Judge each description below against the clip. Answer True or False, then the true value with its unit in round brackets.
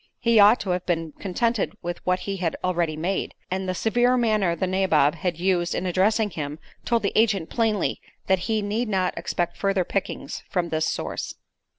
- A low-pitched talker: False (190 Hz)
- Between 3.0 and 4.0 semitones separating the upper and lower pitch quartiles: True (3.5 semitones)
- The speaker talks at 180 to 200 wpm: True (190 wpm)